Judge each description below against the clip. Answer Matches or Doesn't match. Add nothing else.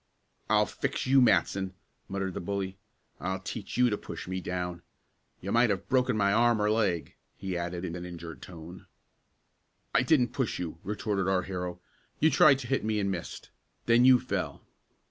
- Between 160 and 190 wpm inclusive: Matches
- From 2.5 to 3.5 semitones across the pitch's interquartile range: Doesn't match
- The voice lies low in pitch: Matches